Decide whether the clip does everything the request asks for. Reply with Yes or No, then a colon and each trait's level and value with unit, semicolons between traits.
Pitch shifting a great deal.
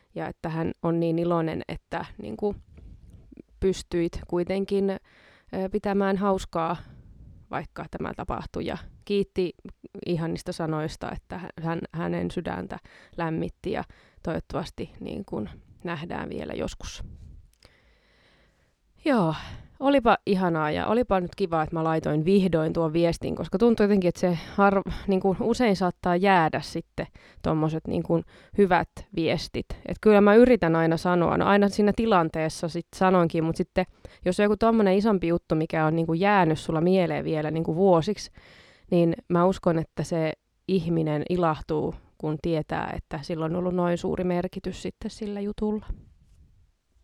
No: average, 3.4 semitones